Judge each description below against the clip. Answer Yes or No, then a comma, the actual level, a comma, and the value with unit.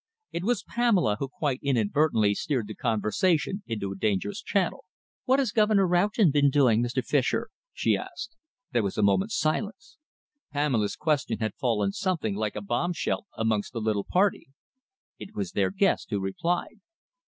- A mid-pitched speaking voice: Yes, medium, 145 Hz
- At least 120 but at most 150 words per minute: No, average, 160 wpm